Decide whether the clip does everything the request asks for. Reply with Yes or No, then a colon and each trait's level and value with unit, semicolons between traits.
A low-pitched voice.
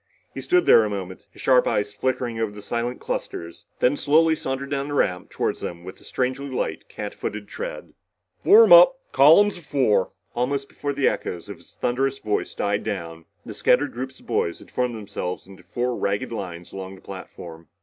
Yes: low, 120 Hz